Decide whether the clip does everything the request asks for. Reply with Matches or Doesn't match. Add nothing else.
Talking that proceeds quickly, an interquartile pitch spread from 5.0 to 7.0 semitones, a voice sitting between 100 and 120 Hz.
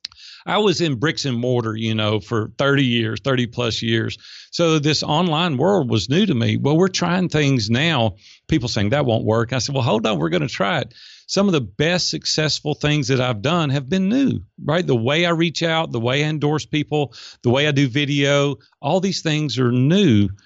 Doesn't match